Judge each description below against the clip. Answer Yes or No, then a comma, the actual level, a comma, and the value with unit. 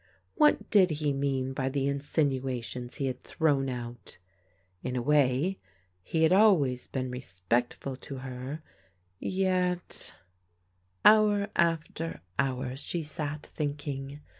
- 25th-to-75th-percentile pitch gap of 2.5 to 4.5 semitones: Yes, average, 4.0 semitones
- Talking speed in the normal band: No, slow, 120 wpm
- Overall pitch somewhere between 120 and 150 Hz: Yes, medium, 140 Hz